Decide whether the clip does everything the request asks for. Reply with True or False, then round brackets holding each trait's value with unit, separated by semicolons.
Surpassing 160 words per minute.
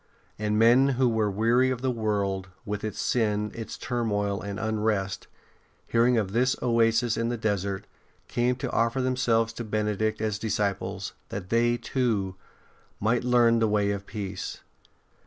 False (155 wpm)